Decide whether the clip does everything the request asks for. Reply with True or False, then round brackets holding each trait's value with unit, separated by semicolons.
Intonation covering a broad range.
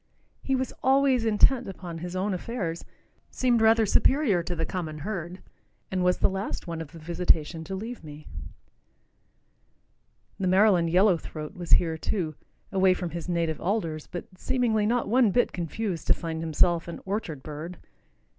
False (4.7 semitones)